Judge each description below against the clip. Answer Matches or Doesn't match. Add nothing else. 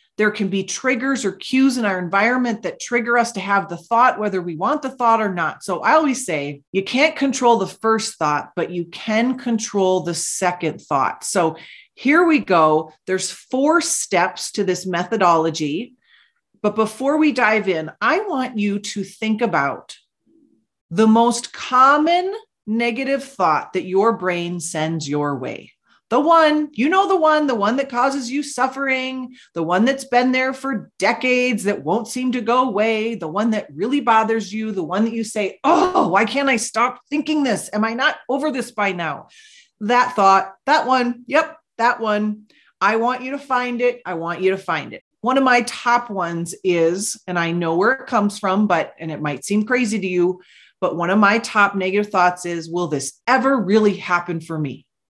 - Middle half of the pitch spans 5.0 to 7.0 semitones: Matches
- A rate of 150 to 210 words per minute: Matches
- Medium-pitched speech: Doesn't match